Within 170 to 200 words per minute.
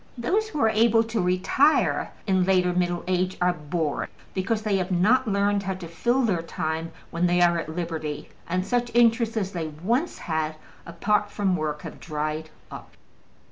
Yes: average, 180 wpm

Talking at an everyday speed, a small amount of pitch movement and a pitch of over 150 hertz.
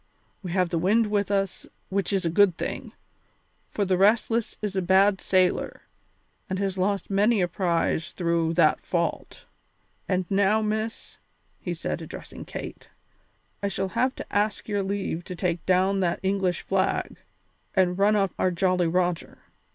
Yes: average, 160 wpm; narrow, 2.1 semitones; high, 190 Hz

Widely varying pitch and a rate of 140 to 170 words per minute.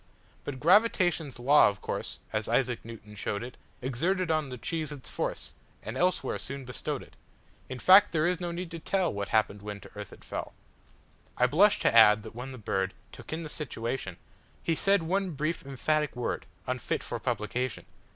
Yes: wide, 6.3 semitones; average, 160 wpm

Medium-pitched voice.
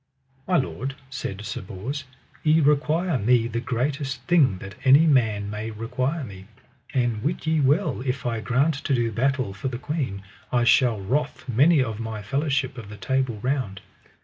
No: low, 130 Hz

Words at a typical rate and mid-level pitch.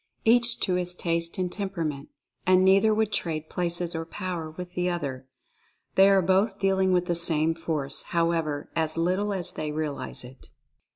Yes: average, 180 wpm; medium, 175 Hz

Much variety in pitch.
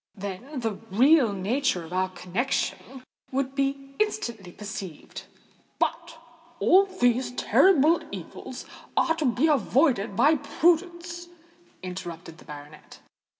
Yes: wide, 8.3 semitones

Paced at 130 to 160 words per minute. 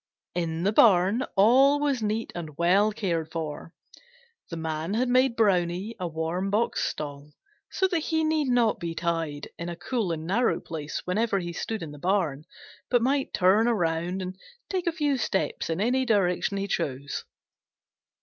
No: average, 170 wpm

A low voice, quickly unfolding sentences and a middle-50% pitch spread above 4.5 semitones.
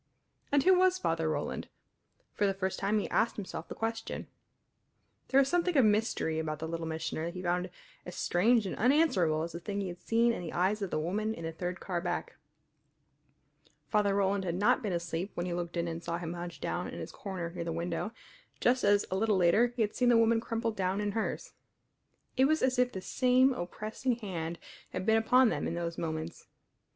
No: high, 195 Hz; fast, 215 wpm; average, 4.9 semitones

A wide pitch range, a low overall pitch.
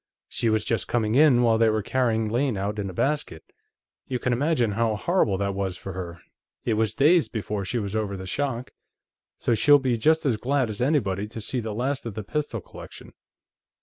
No: average, 4.1 semitones; low, 115 Hz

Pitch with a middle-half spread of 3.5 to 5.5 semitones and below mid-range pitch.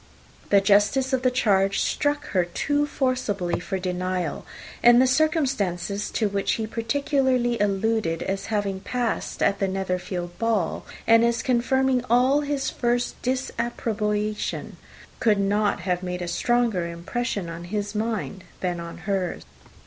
No: average, 4.5 semitones; high, 210 Hz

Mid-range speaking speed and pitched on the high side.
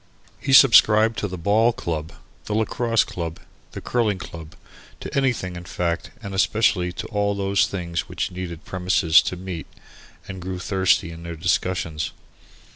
No: average, 160 wpm; very low, 95 Hz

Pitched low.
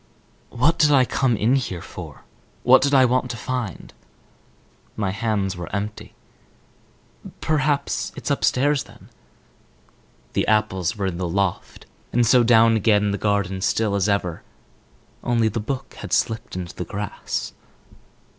Yes: low, 110 Hz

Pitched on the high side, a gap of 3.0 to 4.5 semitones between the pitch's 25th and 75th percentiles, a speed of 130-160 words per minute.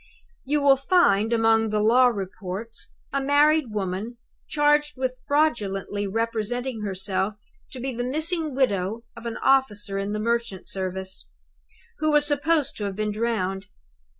No: high, 230 Hz; average, 5.2 semitones; average, 145 wpm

